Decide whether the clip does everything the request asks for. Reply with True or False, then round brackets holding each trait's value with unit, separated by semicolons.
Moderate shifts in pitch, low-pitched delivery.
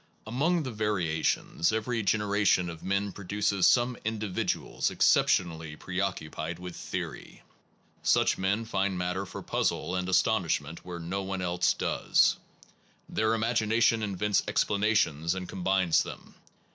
True (3.4 semitones; 95 Hz)